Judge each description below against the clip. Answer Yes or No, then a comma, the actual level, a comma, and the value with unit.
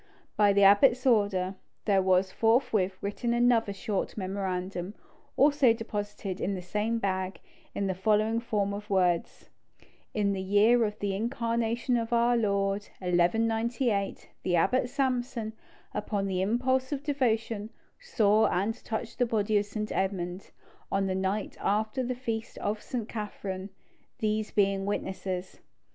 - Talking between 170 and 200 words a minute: No, average, 140 wpm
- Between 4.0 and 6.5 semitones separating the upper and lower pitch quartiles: No, average, 3.0 semitones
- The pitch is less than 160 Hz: No, high, 210 Hz